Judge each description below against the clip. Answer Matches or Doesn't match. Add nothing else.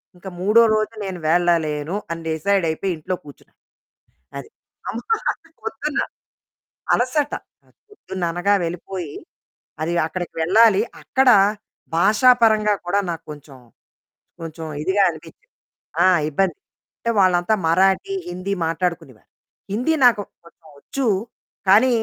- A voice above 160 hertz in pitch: Matches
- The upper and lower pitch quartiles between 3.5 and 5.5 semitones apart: Matches